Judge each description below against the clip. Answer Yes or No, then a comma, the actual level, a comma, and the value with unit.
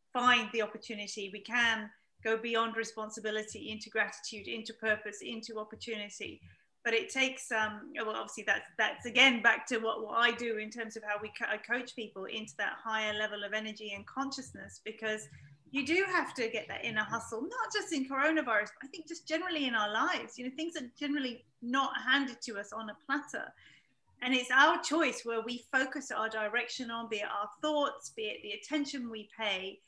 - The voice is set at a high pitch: Yes, high, 230 Hz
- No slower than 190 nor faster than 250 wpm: Yes, average, 200 wpm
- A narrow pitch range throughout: No, average, 3.9 semitones